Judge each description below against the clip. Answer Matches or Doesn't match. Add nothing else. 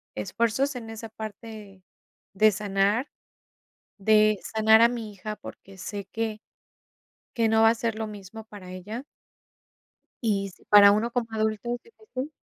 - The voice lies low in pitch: Doesn't match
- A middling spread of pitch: Doesn't match